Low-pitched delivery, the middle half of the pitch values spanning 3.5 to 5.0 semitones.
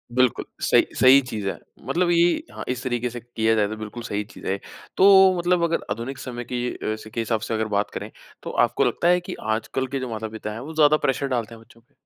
Yes: low, 120 Hz; average, 3.8 semitones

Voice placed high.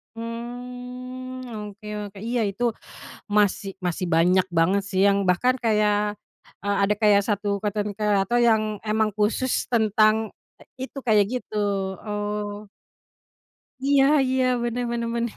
Yes: high, 215 Hz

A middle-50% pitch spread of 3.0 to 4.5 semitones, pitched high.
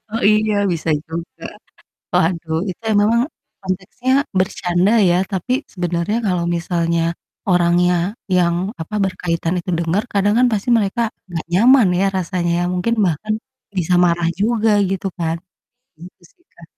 No: average, 3.6 semitones; medium, 180 Hz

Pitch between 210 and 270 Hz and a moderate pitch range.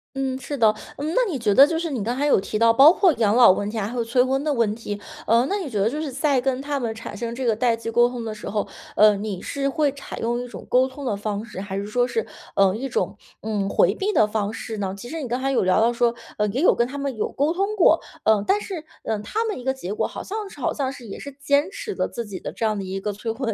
Yes: high, 240 Hz; average, 4.8 semitones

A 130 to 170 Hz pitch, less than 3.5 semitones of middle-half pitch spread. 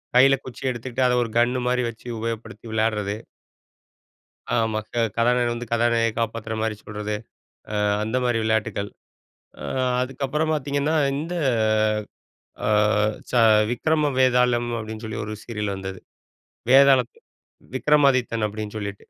No: low, 120 Hz; average, 2.8 semitones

